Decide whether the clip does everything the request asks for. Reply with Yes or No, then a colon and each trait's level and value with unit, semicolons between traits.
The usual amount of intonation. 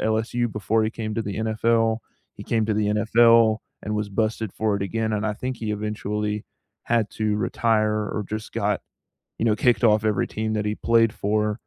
No: narrow, 1.1 semitones